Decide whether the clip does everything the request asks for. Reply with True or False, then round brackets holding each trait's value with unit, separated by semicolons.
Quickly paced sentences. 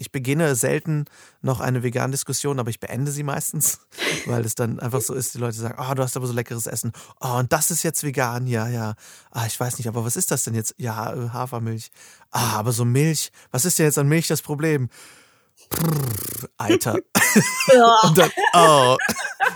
True (195 wpm)